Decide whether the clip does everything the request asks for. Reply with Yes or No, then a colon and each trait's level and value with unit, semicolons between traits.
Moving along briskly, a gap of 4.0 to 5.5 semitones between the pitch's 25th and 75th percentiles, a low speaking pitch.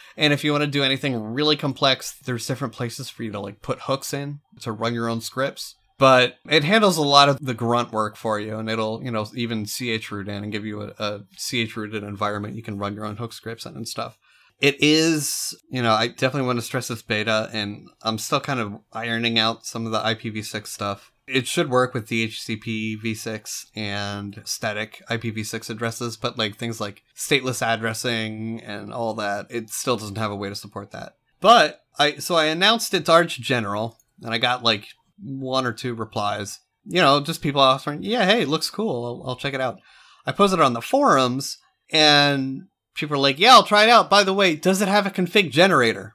Yes: fast, 215 wpm; average, 4.5 semitones; low, 120 Hz